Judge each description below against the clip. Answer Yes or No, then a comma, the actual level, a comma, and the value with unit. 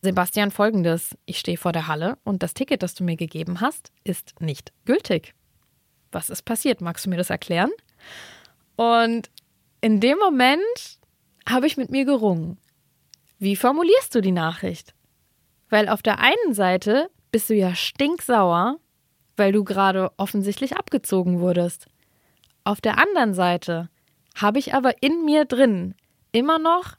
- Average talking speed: Yes, average, 150 wpm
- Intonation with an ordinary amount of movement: No, wide, 6.5 semitones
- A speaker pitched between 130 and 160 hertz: No, high, 210 Hz